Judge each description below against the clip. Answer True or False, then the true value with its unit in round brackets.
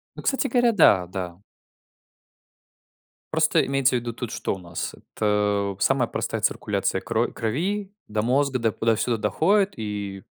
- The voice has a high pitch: False (115 Hz)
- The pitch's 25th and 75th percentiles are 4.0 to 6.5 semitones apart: True (5.1 semitones)